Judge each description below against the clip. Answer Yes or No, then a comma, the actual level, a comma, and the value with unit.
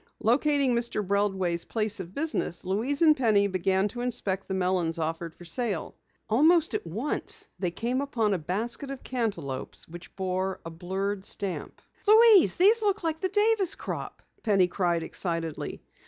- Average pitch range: No, wide, 7.5 semitones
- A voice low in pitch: No, high, 205 Hz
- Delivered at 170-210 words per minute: No, average, 155 wpm